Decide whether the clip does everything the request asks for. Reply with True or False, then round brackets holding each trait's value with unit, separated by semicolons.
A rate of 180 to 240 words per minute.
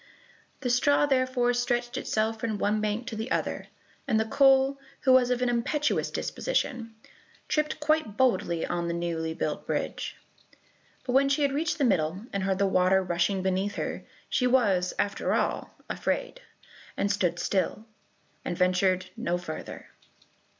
False (160 wpm)